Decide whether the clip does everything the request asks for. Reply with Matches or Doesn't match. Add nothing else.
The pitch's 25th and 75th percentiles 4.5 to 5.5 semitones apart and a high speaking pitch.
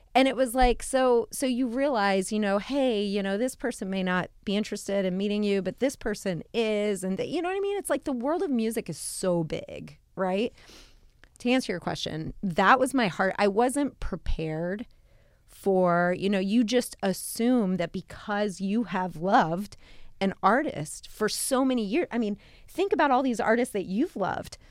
Matches